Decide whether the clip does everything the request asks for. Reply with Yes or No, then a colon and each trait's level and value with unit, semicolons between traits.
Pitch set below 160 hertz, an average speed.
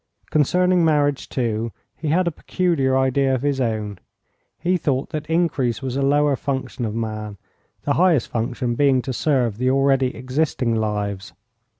Yes: low, 135 Hz; average, 160 wpm